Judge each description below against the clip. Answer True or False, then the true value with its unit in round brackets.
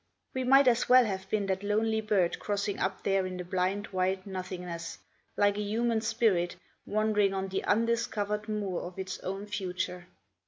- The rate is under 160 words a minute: False (170 wpm)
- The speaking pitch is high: True (200 Hz)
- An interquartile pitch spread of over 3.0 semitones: False (2.4 semitones)